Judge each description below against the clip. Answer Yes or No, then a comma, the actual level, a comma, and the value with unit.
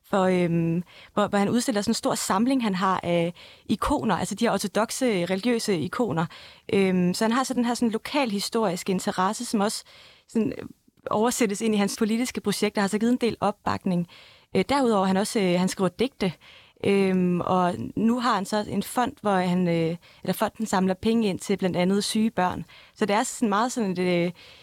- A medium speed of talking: Yes, average, 200 wpm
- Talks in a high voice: Yes, high, 205 Hz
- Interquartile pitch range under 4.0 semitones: Yes, average, 3.6 semitones